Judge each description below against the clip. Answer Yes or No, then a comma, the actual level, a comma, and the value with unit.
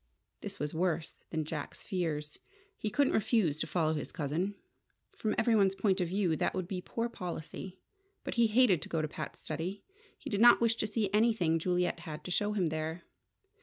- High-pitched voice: No, medium, 180 Hz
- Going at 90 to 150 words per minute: No, average, 195 wpm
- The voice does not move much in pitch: No, average, 4.8 semitones